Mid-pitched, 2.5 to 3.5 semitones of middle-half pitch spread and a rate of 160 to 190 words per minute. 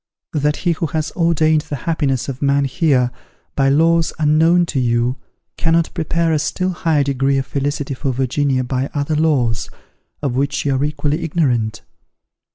Yes: medium, 145 Hz; average, 3.1 semitones; average, 165 wpm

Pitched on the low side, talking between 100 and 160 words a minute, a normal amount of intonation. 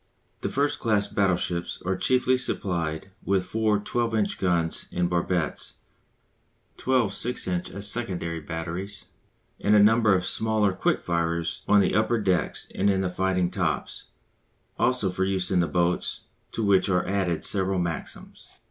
Yes: very low, 95 Hz; average, 155 wpm; average, 3.0 semitones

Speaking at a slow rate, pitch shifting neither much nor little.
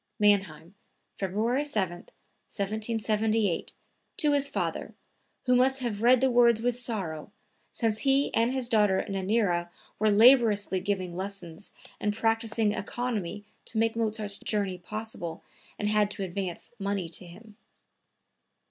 Yes: slow, 130 wpm; average, 3.1 semitones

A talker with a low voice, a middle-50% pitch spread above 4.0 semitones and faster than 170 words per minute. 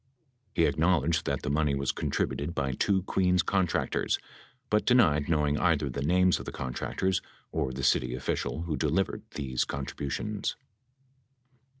No: very low, 75 Hz; average, 4.7 semitones; average, 140 wpm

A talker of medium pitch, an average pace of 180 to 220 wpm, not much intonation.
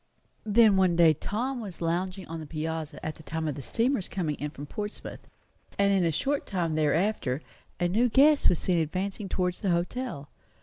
No: medium, 180 Hz; average, 190 wpm; average, 4.5 semitones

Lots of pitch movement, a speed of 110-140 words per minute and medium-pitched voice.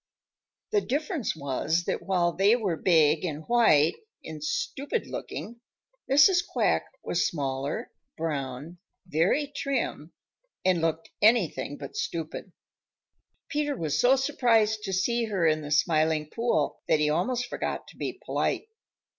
Yes: wide, 7.6 semitones; slow, 135 wpm; medium, 175 Hz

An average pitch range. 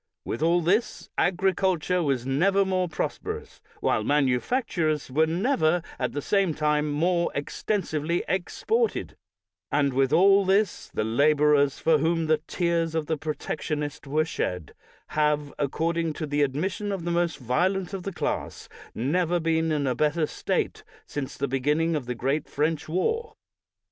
Yes: average, 3.4 semitones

